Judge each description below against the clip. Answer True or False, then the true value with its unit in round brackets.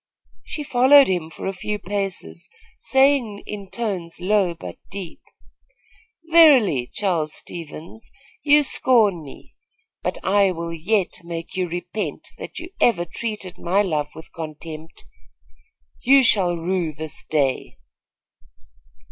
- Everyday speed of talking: False (120 wpm)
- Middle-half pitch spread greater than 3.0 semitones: True (4.8 semitones)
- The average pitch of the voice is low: False (185 Hz)